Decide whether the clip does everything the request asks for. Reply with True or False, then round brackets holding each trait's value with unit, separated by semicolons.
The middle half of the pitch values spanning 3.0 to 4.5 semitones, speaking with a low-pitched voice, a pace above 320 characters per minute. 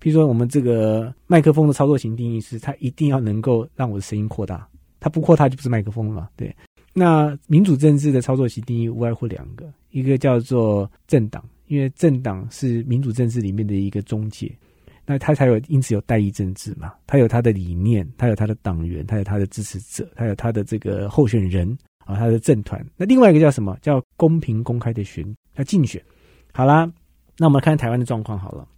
False (4.9 semitones; 120 Hz; 330 characters per minute)